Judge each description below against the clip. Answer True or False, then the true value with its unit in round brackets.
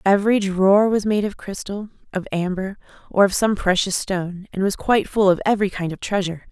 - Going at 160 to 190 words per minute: False (205 wpm)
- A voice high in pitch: True (195 Hz)